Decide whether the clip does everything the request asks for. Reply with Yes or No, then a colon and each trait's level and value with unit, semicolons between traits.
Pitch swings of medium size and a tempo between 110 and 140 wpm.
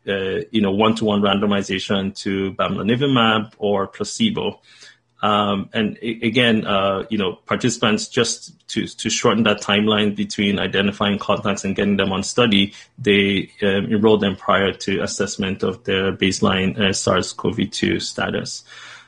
No: narrow, 2.0 semitones; slow, 135 wpm